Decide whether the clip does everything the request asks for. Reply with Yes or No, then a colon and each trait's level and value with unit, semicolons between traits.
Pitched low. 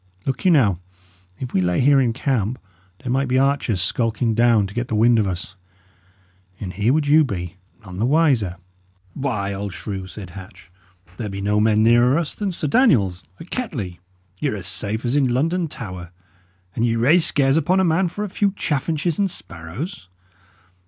Yes: low, 120 Hz